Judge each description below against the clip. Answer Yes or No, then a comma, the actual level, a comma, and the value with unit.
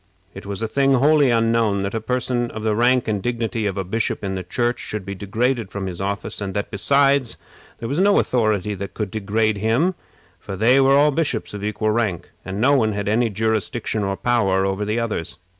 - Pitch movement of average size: Yes, average, 3.3 semitones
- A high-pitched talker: No, low, 110 Hz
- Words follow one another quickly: Yes, fast, 215 wpm